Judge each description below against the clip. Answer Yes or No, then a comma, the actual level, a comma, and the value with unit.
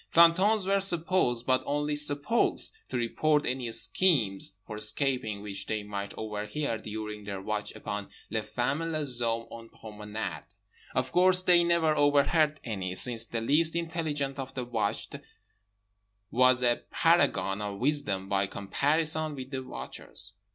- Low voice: Yes, low, 130 Hz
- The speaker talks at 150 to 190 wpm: No, average, 140 wpm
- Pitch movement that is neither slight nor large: No, wide, 6.4 semitones